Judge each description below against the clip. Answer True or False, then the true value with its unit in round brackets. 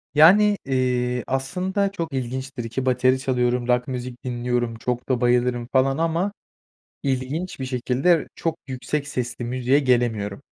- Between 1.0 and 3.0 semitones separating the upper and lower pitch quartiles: True (2.5 semitones)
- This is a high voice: False (130 Hz)